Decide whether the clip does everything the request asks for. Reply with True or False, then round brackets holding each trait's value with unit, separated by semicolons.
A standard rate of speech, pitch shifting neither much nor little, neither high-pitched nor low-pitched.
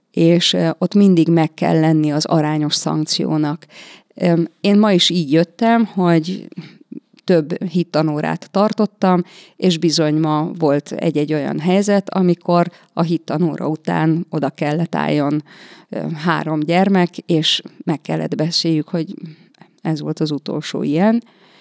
True (120 wpm; 3.0 semitones; 170 Hz)